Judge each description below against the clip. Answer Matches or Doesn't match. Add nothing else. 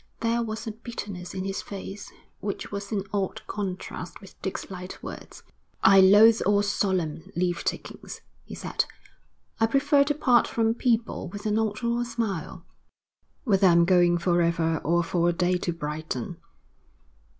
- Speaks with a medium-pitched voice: Doesn't match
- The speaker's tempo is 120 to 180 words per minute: Matches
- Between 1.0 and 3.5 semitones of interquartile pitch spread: Doesn't match